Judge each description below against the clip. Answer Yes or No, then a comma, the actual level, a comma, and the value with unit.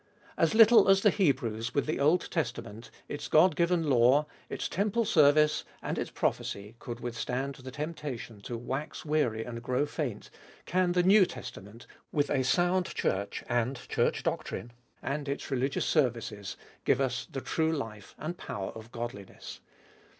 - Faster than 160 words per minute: No, average, 155 wpm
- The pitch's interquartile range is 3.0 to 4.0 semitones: No, average, 5.2 semitones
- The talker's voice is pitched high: No, low, 135 Hz